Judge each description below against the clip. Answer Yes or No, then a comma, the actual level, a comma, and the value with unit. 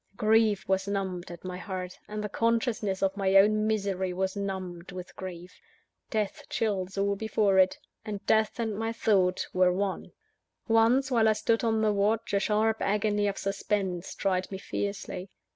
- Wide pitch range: No, narrow, 2.4 semitones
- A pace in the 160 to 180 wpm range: Yes, average, 175 wpm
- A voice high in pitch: Yes, high, 200 Hz